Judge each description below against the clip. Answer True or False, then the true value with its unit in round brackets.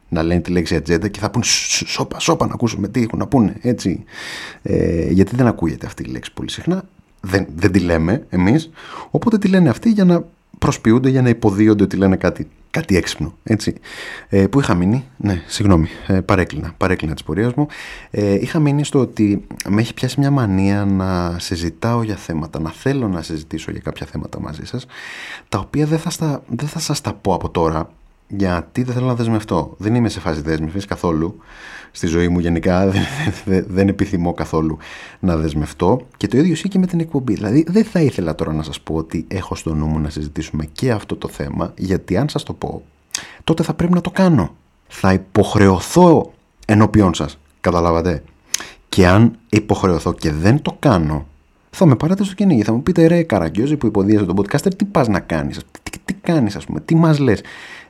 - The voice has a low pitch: True (100 Hz)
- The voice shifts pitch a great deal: True (7.7 semitones)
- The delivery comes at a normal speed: False (200 wpm)